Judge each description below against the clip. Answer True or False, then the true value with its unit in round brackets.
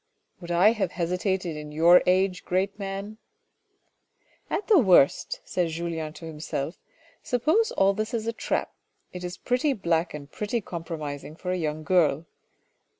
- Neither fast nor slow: True (170 wpm)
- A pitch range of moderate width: True (3.9 semitones)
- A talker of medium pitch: True (180 Hz)